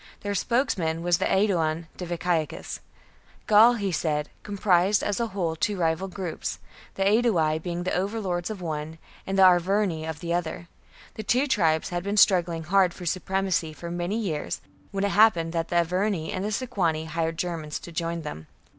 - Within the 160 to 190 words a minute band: Yes, average, 175 wpm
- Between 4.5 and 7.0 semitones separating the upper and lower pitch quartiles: No, average, 3.4 semitones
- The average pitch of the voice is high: No, medium, 175 Hz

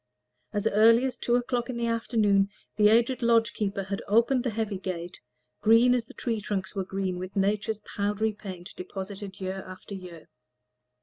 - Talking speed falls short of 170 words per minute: No, average, 175 wpm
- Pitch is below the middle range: No, high, 210 Hz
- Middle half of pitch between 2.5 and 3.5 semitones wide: Yes, average, 3.1 semitones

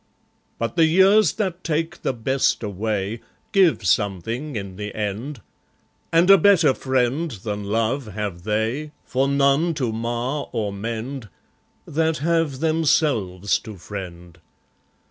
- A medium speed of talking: No, slow, 125 wpm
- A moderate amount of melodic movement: No, wide, 7.0 semitones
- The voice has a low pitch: Yes, low, 125 Hz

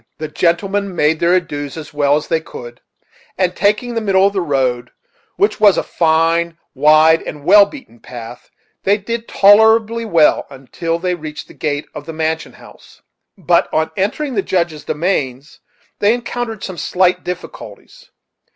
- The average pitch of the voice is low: No, medium, 170 Hz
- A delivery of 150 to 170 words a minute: Yes, average, 160 wpm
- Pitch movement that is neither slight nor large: Yes, average, 4.8 semitones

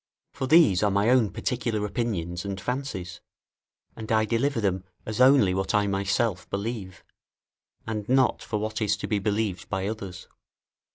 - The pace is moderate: Yes, average, 160 wpm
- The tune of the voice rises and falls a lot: No, average, 3.1 semitones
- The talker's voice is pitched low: Yes, low, 105 Hz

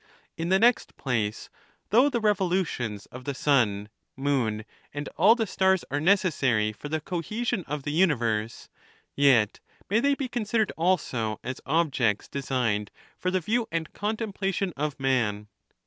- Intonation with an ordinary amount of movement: No, wide, 7.9 semitones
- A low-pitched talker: No, medium, 150 Hz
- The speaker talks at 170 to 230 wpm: No, average, 145 wpm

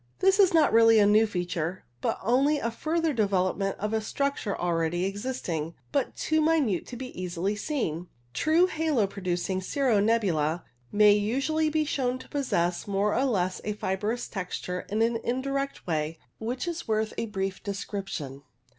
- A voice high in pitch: Yes, high, 210 Hz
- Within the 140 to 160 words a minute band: No, average, 170 wpm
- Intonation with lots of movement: Yes, wide, 6.4 semitones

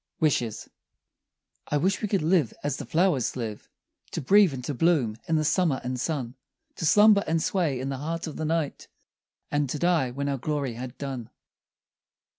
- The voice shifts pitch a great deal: No, average, 4.4 semitones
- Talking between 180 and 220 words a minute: Yes, average, 185 wpm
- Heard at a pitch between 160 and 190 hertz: No, medium, 145 Hz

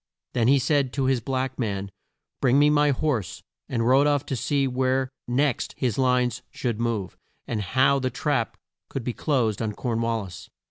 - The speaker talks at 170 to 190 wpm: Yes, average, 185 wpm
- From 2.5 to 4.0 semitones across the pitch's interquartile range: Yes, average, 2.8 semitones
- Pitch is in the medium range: No, low, 130 Hz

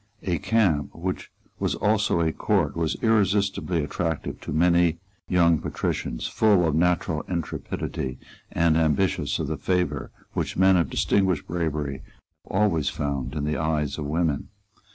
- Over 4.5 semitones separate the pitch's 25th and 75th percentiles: No, average, 3.5 semitones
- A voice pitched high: No, very low, 85 Hz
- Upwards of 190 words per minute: No, average, 145 wpm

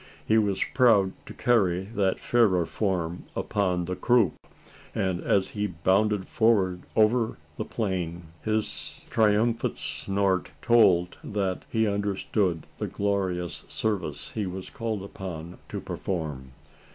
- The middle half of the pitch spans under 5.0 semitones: Yes, average, 3.3 semitones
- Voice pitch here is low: Yes, low, 100 Hz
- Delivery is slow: Yes, slow, 125 wpm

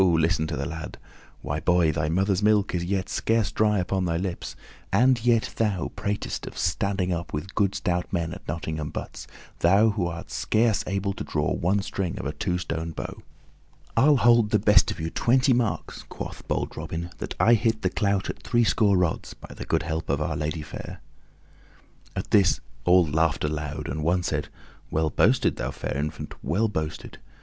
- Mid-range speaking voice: No, very low, 90 Hz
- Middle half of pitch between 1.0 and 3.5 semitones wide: No, average, 4.3 semitones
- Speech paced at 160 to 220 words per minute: Yes, average, 190 wpm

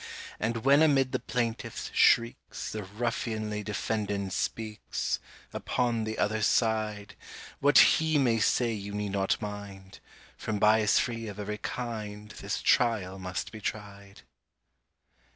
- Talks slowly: Yes, slow, 130 wpm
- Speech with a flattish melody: Yes, narrow, 2.2 semitones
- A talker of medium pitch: No, low, 110 Hz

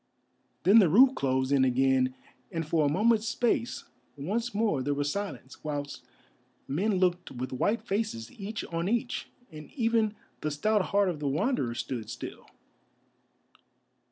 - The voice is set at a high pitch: No, medium, 175 Hz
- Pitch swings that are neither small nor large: No, wide, 7.7 semitones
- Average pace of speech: Yes, average, 150 wpm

